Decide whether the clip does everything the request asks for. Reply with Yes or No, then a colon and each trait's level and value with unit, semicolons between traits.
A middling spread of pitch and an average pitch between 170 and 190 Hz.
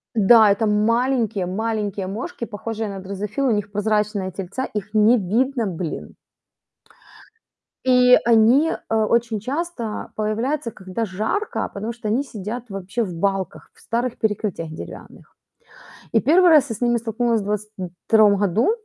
No: average, 3.0 semitones; high, 220 Hz